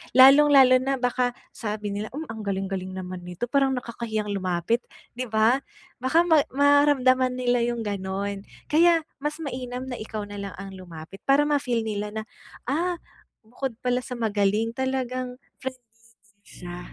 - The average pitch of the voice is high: Yes, high, 240 Hz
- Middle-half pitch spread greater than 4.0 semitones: Yes, average, 4.4 semitones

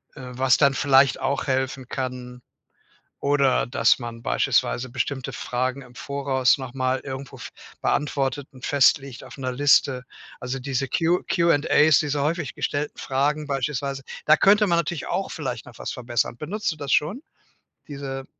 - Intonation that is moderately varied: No, narrow, 2.1 semitones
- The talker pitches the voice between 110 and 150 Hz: Yes, low, 135 Hz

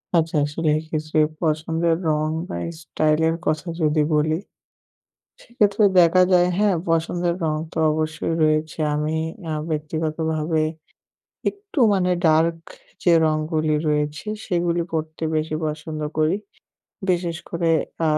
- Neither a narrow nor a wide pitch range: No, narrow, 1.6 semitones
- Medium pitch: Yes, medium, 160 Hz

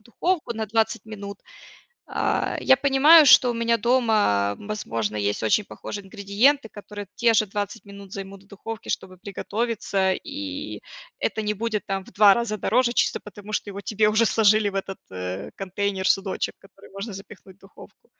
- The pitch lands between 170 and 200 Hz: No, high, 210 Hz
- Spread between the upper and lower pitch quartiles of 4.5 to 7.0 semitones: No, average, 2.8 semitones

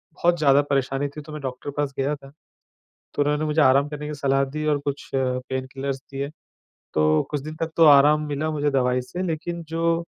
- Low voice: No, medium, 145 Hz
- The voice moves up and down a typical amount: No, narrow, 2.0 semitones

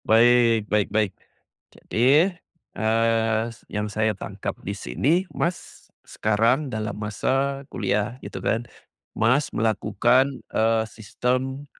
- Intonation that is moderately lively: Yes, average, 3.1 semitones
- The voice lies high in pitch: No, low, 115 Hz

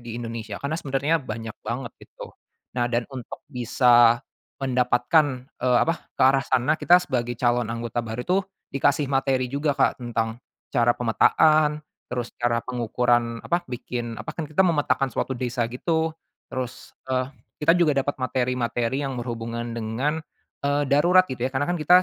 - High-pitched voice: No, low, 125 Hz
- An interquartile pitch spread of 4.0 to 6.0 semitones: No, average, 3.4 semitones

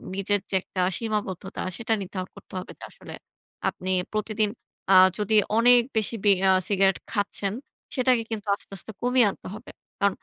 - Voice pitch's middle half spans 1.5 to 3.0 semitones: Yes, narrow, 2.5 semitones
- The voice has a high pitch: Yes, high, 210 Hz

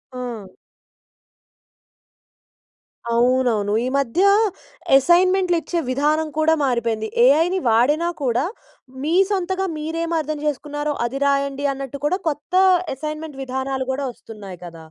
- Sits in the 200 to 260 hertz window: No, very high, 280 Hz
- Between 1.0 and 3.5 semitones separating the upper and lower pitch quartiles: No, average, 4.0 semitones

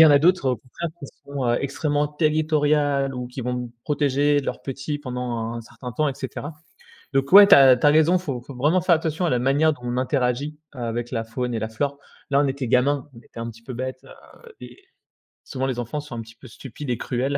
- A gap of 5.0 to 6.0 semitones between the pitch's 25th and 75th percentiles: No, average, 3.0 semitones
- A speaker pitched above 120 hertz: Yes, low, 135 Hz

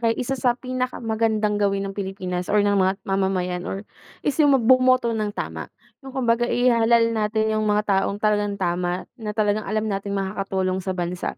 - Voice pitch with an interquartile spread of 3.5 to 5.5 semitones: No, average, 3.1 semitones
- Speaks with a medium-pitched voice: No, high, 210 Hz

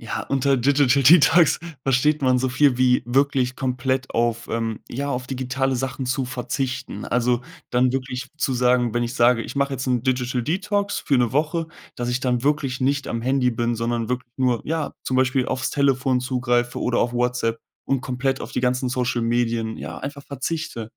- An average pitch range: No, narrow, 1.8 semitones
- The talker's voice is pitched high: No, low, 130 Hz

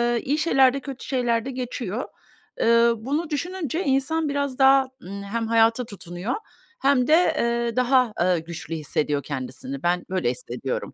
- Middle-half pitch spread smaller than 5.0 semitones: No, wide, 5.5 semitones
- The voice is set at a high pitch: Yes, high, 240 Hz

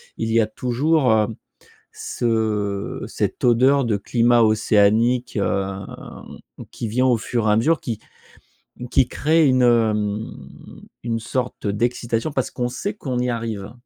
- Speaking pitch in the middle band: No, low, 115 Hz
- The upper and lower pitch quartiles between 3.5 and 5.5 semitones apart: No, average, 2.7 semitones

